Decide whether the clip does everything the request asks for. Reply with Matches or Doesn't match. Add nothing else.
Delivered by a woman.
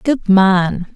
Matches